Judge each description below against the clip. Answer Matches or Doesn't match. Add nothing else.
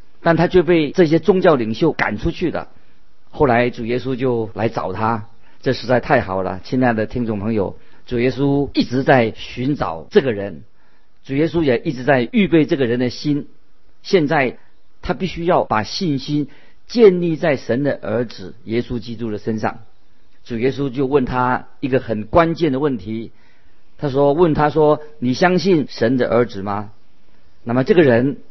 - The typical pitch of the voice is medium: Doesn't match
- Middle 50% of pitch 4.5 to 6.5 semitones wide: Matches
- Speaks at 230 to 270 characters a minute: Matches